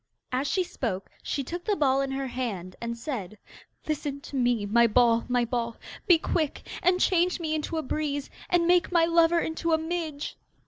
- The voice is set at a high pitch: Yes, very high, 285 Hz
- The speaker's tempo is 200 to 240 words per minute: No, average, 190 wpm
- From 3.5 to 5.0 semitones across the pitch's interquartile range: No, wide, 5.6 semitones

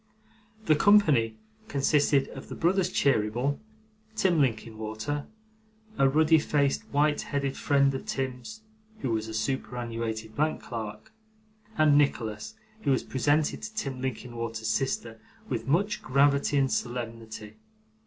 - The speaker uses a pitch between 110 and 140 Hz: Yes, low, 135 Hz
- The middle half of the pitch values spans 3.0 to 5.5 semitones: Yes, average, 4.4 semitones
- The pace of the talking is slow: Yes, slow, 125 wpm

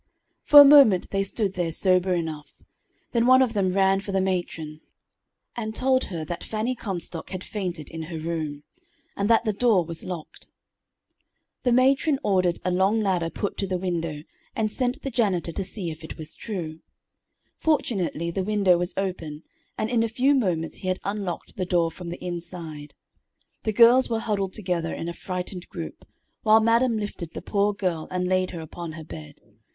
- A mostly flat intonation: No, average, 4.3 semitones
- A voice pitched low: No, medium, 185 Hz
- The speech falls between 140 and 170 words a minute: No, average, 185 wpm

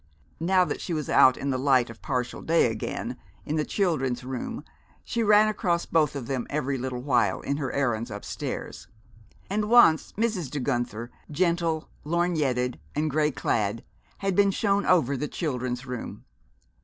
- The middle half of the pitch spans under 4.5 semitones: No, wide, 5.5 semitones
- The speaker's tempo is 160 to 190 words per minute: Yes, average, 165 wpm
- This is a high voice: No, medium, 145 Hz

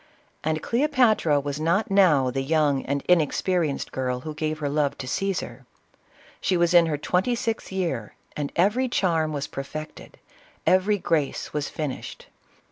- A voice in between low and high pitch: Yes, medium, 155 Hz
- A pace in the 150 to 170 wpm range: Yes, average, 155 wpm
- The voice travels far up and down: No, average, 4.7 semitones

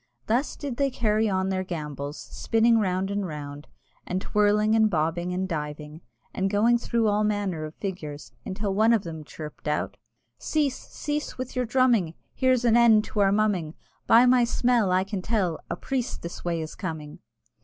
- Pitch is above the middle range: Yes, high, 200 Hz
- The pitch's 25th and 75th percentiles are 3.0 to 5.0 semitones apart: No, wide, 5.5 semitones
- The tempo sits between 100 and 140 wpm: No, average, 180 wpm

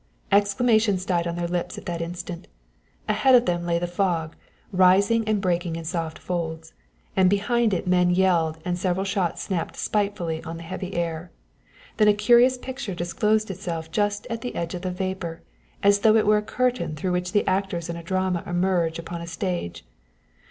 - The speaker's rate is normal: Yes, average, 185 wpm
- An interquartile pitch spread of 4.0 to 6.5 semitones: No, average, 3.1 semitones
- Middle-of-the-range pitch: Yes, medium, 180 Hz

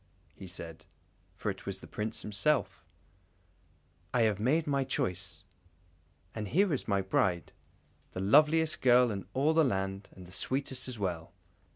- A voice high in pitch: No, low, 110 Hz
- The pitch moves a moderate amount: No, wide, 6.2 semitones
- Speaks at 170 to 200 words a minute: No, average, 155 wpm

